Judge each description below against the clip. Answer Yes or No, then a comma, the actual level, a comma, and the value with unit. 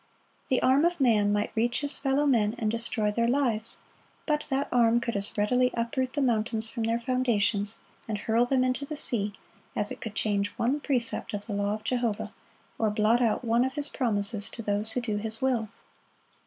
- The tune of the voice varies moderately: Yes, average, 3.2 semitones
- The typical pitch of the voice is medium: No, high, 230 Hz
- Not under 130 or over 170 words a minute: No, average, 200 wpm